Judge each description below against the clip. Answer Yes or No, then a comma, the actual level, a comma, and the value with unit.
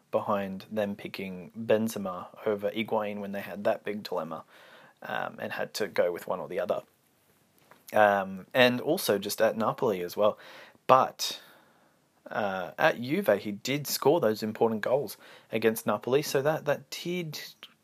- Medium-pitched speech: No, low, 110 Hz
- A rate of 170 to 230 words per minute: No, average, 155 wpm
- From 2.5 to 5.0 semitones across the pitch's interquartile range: Yes, average, 4.3 semitones